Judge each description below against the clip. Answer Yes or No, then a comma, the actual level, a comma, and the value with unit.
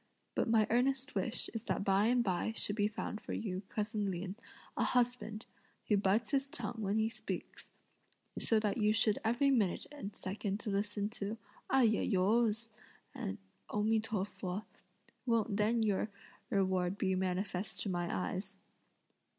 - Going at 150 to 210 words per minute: Yes, average, 160 wpm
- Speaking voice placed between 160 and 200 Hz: No, high, 210 Hz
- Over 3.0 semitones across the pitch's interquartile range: No, narrow, 2.5 semitones